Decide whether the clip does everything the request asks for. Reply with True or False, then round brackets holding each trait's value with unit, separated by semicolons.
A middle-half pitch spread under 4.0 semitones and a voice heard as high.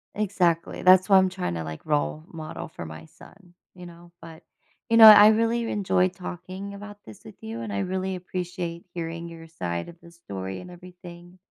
False (2.9 semitones; 175 Hz)